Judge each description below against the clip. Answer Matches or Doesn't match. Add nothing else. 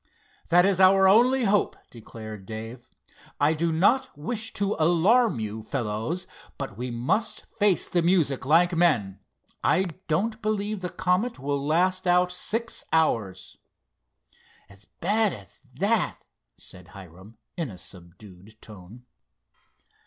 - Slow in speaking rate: Matches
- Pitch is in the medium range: Matches